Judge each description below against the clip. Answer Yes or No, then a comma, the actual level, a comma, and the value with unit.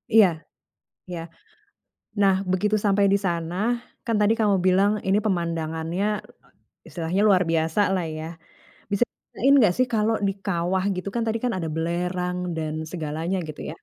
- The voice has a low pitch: No, medium, 185 Hz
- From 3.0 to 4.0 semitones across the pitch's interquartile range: Yes, average, 3.4 semitones